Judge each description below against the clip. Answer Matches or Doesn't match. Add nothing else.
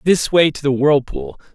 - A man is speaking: Matches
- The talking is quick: Doesn't match